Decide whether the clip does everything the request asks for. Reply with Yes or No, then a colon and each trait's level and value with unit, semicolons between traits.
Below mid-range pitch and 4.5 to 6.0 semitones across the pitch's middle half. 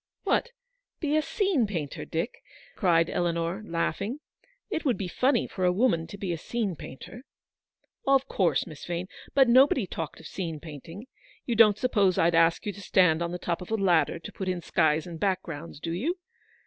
No: medium, 185 Hz; wide, 5.4 semitones